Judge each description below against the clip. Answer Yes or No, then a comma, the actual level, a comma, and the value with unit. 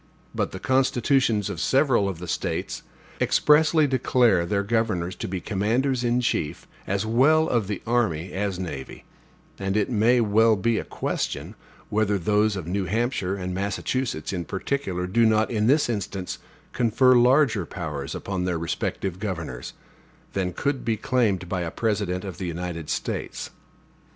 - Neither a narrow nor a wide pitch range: Yes, average, 4.8 semitones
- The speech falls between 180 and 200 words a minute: No, average, 155 wpm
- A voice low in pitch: Yes, low, 105 Hz